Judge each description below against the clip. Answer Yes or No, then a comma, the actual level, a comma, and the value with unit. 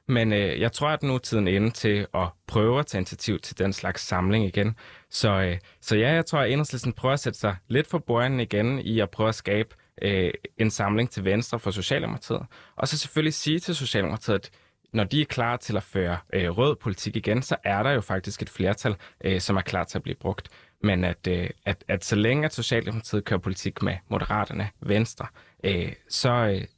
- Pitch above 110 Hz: No, low, 105 Hz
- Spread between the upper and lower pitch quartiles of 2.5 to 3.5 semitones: No, average, 3.9 semitones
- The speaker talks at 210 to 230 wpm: Yes, average, 220 wpm